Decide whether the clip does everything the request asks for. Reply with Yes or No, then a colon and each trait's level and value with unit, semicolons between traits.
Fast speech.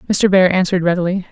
No: average, 180 wpm